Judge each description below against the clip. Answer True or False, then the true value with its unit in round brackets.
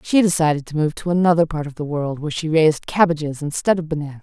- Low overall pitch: False (155 Hz)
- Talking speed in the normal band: False (240 wpm)